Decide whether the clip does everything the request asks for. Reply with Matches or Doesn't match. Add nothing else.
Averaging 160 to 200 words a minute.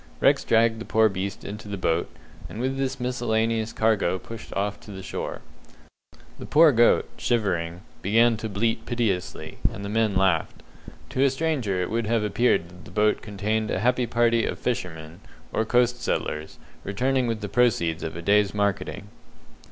Matches